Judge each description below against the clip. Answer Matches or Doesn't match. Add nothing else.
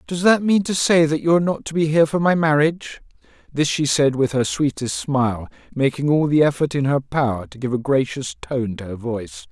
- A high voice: Doesn't match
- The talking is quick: Matches